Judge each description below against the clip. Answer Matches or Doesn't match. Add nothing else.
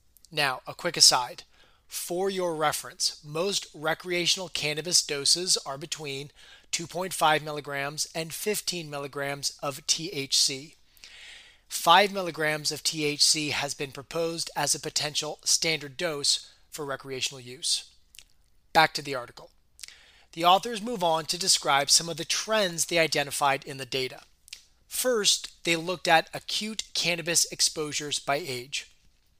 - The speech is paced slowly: Matches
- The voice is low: Doesn't match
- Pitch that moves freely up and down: Doesn't match